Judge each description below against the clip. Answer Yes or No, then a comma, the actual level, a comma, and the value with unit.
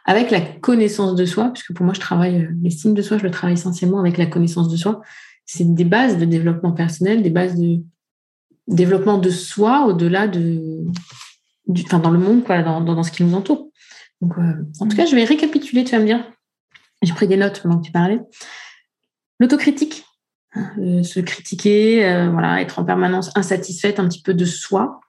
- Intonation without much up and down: No, average, 3.4 semitones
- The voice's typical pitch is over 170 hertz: Yes, medium, 185 Hz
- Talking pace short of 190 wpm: No, average, 200 wpm